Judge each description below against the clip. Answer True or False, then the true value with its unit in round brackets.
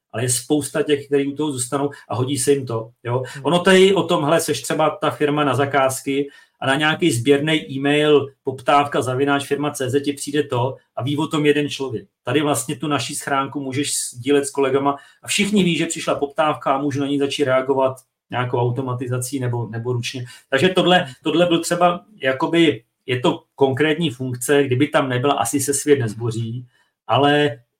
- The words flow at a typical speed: False (185 wpm)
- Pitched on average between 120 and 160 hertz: True (140 Hz)